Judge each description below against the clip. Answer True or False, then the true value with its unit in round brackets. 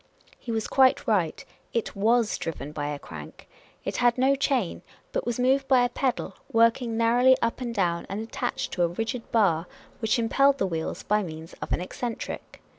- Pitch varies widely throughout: True (5.7 semitones)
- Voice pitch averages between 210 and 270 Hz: True (225 Hz)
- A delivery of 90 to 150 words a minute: False (190 wpm)